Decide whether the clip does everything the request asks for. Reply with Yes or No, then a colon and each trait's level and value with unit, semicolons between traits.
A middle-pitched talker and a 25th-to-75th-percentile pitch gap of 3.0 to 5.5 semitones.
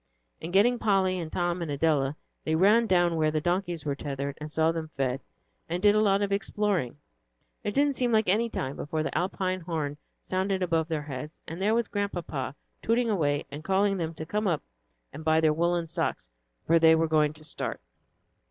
Yes: medium, 170 Hz; average, 4.2 semitones